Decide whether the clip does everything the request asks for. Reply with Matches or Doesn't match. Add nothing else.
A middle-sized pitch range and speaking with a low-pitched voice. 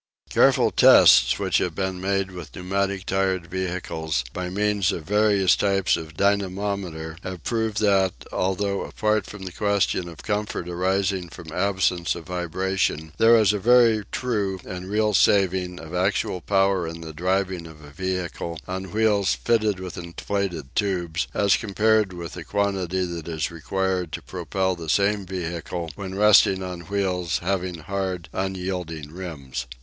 Doesn't match